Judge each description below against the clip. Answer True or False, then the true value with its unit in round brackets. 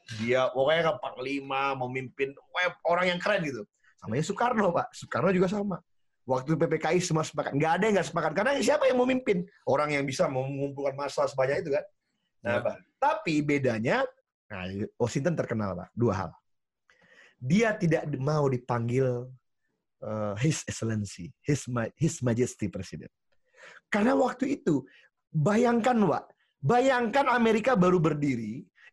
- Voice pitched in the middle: True (150 Hz)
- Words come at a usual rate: False (145 wpm)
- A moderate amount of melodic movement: False (7.6 semitones)